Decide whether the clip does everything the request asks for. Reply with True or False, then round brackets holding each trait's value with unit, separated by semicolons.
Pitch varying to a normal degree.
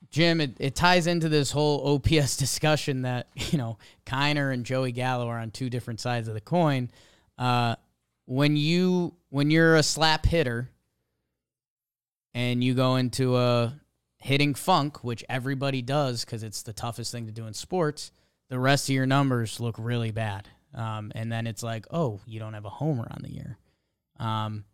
True (4.1 semitones)